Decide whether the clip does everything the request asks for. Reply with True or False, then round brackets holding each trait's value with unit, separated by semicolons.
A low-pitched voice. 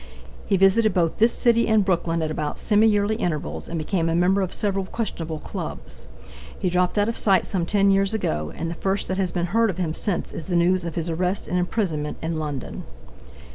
False (180 Hz)